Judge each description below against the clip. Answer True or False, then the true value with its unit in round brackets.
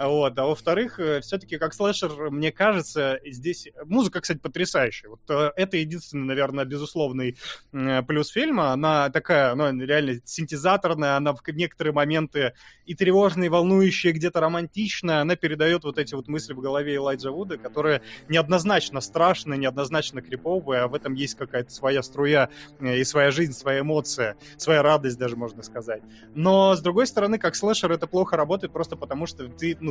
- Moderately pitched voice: True (150 Hz)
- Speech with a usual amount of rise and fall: True (4.0 semitones)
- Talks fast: True (165 wpm)